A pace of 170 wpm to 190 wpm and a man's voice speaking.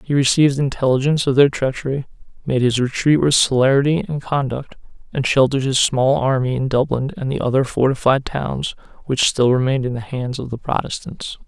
Yes: average, 180 wpm; male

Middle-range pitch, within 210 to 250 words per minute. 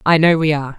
No: medium, 155 Hz; fast, 305 wpm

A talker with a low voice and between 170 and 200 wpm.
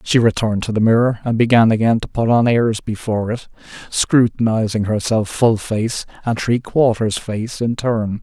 Yes: low, 115 Hz; average, 175 wpm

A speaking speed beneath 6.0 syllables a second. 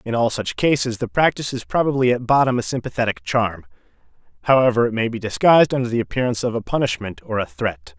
No: 6.5 syllables/s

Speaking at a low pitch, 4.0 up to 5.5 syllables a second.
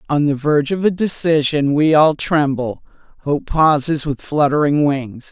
No: medium, 150 Hz; 4.5 syllables/s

